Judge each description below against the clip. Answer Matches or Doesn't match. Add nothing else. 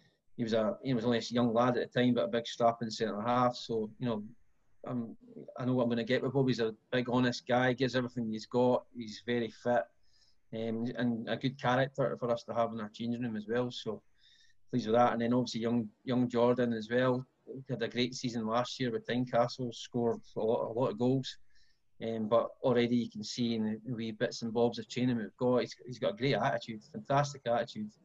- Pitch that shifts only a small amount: Matches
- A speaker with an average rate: Doesn't match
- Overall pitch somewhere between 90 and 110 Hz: Doesn't match